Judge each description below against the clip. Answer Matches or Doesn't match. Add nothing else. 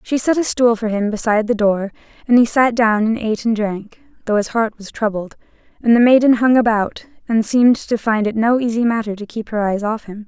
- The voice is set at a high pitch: Matches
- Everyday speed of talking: Doesn't match